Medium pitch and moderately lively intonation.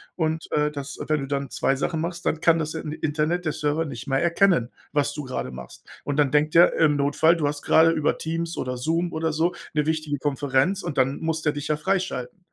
No: medium, 150 Hz; narrow, 2.3 semitones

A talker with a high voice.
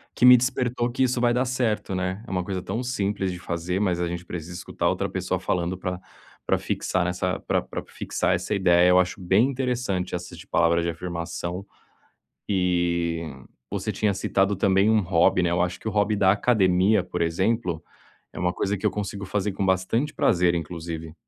No: very low, 95 Hz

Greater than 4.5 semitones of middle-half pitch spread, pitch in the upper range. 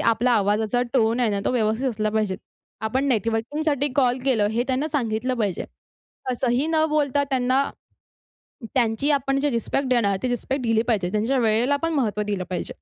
No: average, 3.8 semitones; high, 245 Hz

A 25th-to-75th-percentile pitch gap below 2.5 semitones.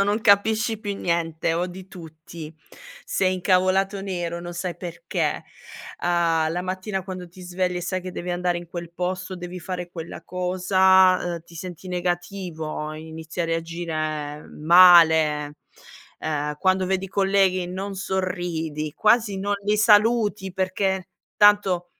Yes: narrow, 2.1 semitones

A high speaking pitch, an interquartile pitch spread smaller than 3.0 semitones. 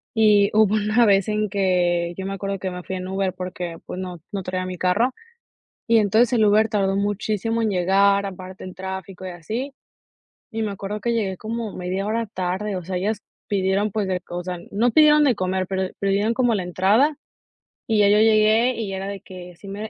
Yes: high, 200 Hz; narrow, 2.6 semitones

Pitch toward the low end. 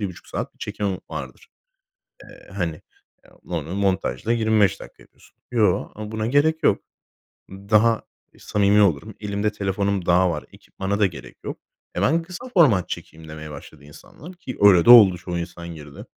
Yes: low, 100 Hz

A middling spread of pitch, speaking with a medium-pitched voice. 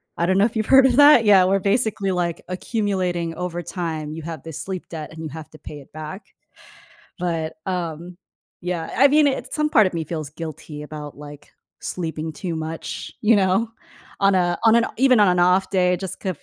Yes: average, 3.7 semitones; medium, 180 Hz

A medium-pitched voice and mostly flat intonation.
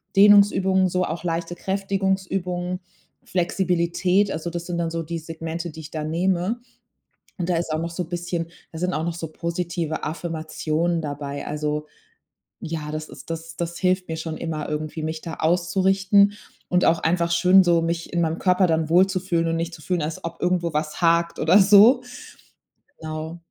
Yes: medium, 170 Hz; narrow, 2.1 semitones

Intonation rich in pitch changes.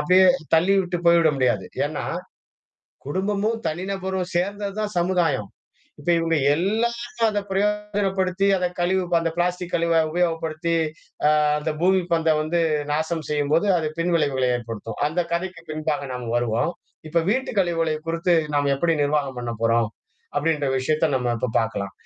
No: average, 4.2 semitones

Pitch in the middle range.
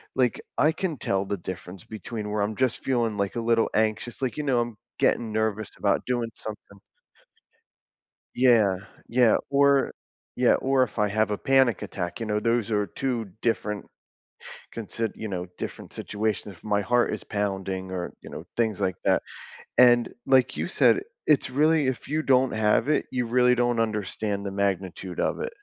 No: low, 110 Hz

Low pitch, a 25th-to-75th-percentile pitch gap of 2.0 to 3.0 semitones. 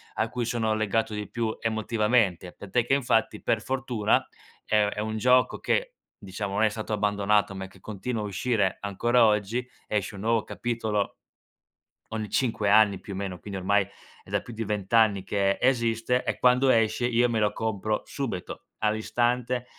Yes: low, 110 Hz; narrow, 2.6 semitones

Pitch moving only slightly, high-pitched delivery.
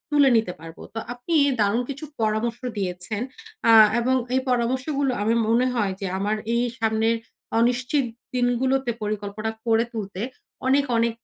No: average, 3.1 semitones; high, 230 Hz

